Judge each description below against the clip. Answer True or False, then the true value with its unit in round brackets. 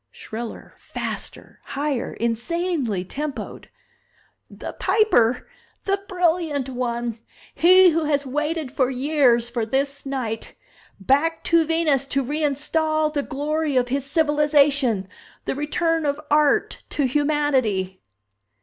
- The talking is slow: True (115 wpm)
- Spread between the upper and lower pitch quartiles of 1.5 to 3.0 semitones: False (3.7 semitones)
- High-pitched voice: True (285 Hz)